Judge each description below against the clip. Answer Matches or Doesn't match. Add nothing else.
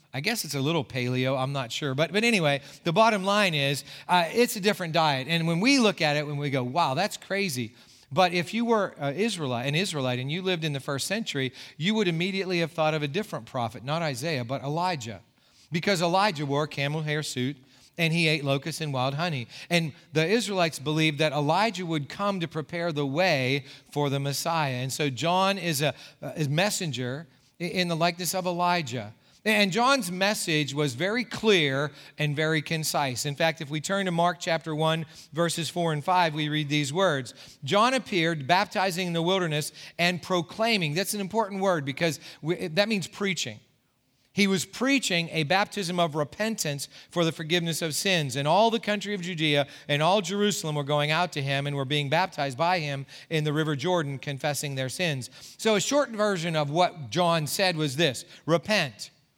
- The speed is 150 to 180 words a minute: Doesn't match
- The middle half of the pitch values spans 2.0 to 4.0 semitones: Doesn't match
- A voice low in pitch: Doesn't match